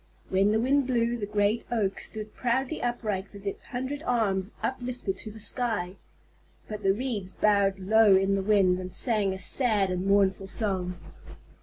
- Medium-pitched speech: No, high, 205 Hz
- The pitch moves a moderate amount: Yes, average, 3.6 semitones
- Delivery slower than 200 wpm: Yes, average, 170 wpm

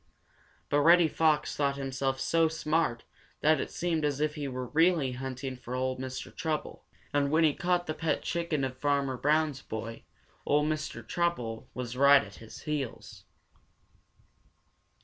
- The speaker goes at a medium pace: Yes, average, 155 wpm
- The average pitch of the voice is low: No, medium, 145 Hz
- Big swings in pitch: No, average, 3.3 semitones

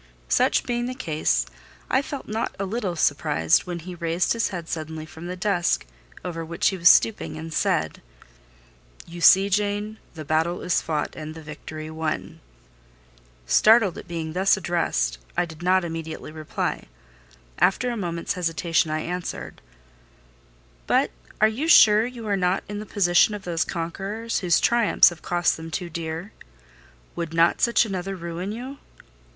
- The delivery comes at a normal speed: Yes, average, 160 wpm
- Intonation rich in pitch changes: No, average, 4.1 semitones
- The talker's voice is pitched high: No, medium, 175 Hz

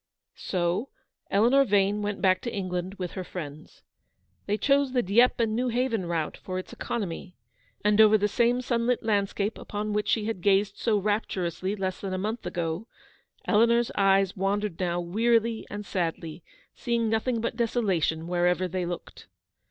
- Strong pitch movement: No, average, 3.7 semitones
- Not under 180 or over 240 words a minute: No, average, 165 wpm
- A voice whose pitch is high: Yes, high, 205 Hz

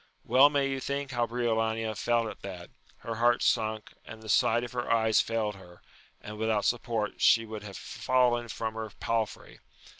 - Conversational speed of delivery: Yes, average, 180 wpm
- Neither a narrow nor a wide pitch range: No, narrow, 1.8 semitones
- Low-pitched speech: Yes, low, 115 Hz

